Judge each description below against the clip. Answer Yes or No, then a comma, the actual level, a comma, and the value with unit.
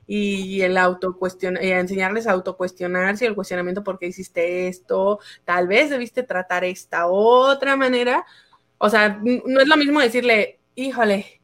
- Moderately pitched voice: No, high, 195 Hz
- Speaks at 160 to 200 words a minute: No, average, 145 wpm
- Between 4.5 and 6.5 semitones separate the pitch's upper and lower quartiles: Yes, average, 4.8 semitones